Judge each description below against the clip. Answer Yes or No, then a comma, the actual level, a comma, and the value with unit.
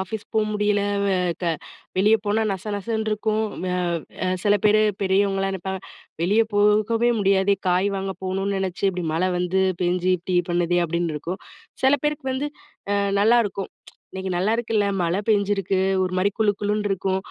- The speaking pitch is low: No, high, 195 Hz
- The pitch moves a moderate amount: No, narrow, 2.2 semitones